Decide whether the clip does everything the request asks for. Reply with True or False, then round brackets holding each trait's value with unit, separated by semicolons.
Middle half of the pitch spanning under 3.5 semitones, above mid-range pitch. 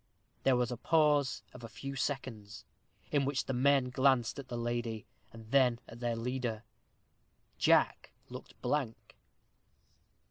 False (2.8 semitones; 125 Hz)